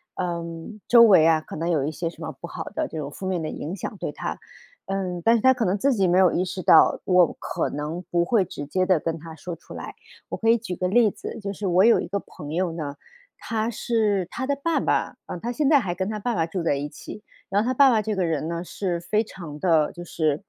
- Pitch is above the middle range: No, medium, 180 Hz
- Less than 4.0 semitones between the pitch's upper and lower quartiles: No, average, 4.5 semitones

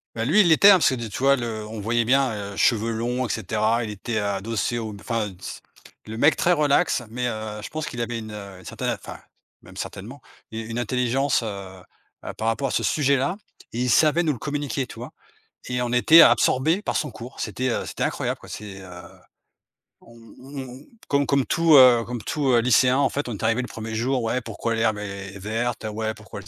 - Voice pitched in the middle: No, low, 120 Hz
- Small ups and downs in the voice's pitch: No, average, 3.7 semitones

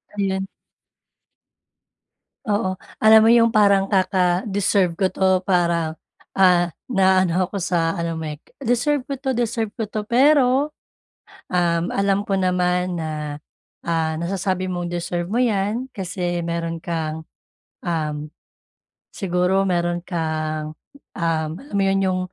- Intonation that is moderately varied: Yes, average, 3.0 semitones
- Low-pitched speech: No, medium, 185 Hz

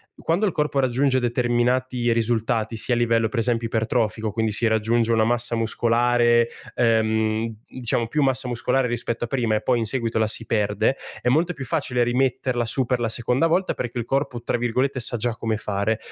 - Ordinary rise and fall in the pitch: No, narrow, 2.1 semitones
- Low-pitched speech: Yes, low, 120 Hz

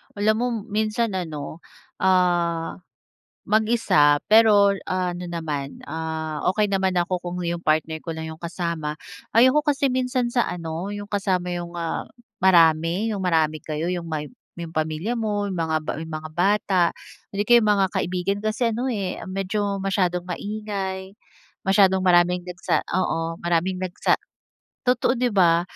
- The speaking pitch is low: No, medium, 185 Hz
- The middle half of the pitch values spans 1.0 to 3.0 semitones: No, average, 3.7 semitones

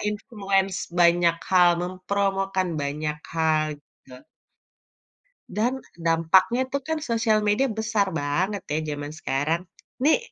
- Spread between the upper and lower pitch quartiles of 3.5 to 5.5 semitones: Yes, average, 4.5 semitones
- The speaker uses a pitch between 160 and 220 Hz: Yes, medium, 185 Hz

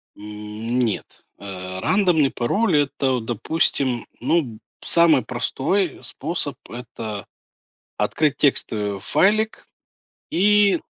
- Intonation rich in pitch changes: Yes, wide, 7.4 semitones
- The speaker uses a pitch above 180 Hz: No, low, 130 Hz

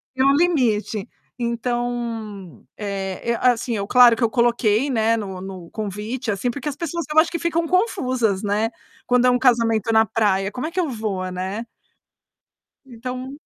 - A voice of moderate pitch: No, high, 235 Hz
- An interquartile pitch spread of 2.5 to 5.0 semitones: Yes, average, 3.6 semitones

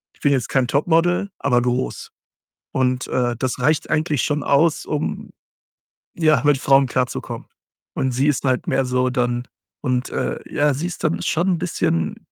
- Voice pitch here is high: No, low, 135 Hz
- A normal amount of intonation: Yes, average, 3.4 semitones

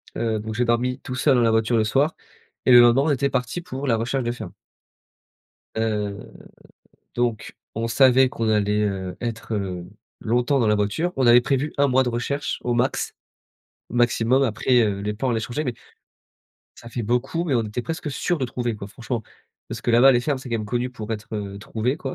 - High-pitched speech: No, low, 120 Hz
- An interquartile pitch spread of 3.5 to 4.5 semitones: No, average, 3.0 semitones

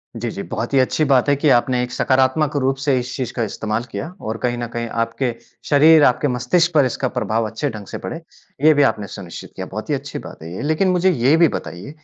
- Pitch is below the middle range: Yes, low, 130 Hz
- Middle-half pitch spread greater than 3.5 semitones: Yes, average, 4.1 semitones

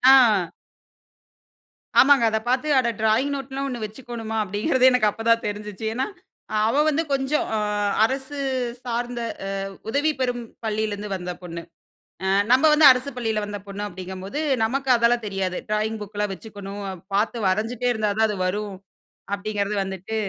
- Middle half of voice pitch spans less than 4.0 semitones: Yes, average, 3.5 semitones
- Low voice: No, high, 220 Hz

